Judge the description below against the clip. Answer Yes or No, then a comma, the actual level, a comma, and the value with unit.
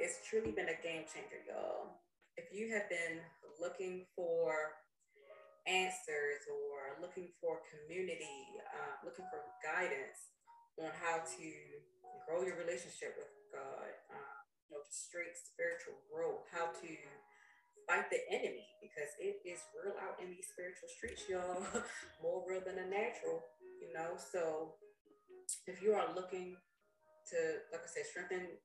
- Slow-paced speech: No, average, 145 wpm